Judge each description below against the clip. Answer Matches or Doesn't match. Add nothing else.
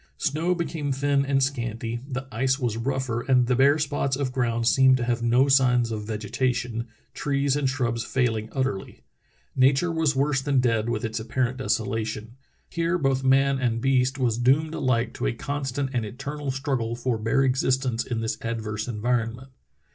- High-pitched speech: Doesn't match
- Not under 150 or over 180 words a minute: Matches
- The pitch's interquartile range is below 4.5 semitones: Matches